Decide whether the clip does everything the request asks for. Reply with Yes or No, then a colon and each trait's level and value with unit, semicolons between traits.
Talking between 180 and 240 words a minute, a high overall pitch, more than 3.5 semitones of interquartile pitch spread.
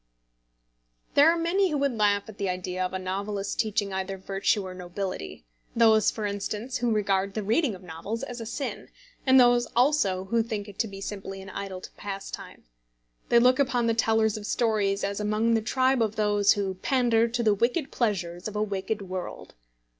No: average, 190 wpm; high, 210 Hz; average, 3.2 semitones